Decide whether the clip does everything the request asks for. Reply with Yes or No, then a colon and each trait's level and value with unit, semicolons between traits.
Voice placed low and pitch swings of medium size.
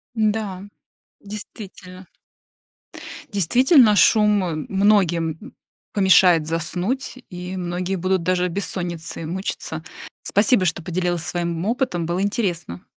No: medium, 185 Hz; average, 3.0 semitones